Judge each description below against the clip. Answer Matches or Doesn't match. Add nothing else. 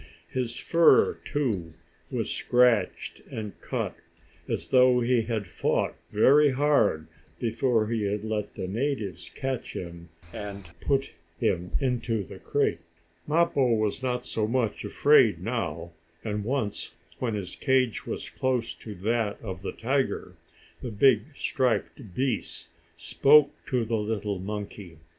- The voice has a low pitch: Matches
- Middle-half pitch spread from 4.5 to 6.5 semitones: Doesn't match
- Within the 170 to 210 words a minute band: Doesn't match